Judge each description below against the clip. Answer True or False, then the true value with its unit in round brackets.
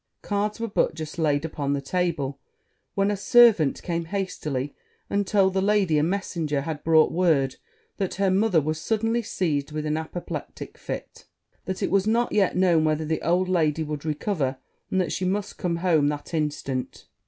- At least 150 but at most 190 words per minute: True (180 wpm)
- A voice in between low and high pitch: True (170 Hz)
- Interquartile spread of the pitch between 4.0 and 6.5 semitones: True (4.3 semitones)